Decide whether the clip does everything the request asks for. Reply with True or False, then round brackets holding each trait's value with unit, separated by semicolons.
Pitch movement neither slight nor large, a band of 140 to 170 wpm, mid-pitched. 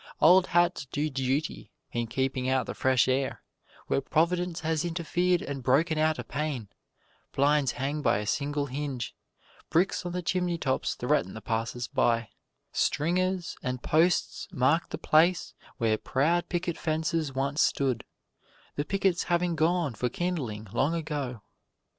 True (4.7 semitones; 145 wpm; 150 Hz)